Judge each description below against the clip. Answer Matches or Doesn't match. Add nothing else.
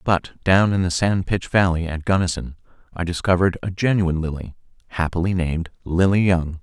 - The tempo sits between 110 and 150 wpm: Doesn't match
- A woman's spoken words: Doesn't match